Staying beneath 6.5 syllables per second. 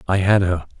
Yes: 5.5 syllables/s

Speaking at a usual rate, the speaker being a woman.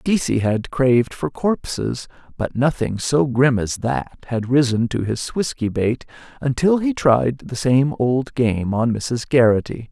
No: average, 165 wpm; male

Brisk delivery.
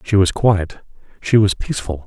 No: average, 175 wpm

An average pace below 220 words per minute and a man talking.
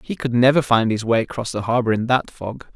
No: fast, 260 wpm; male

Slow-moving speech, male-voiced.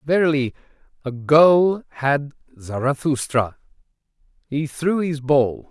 Yes: slow, 95 wpm; male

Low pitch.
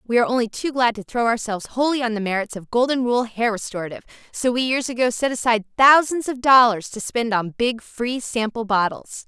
No: high, 235 Hz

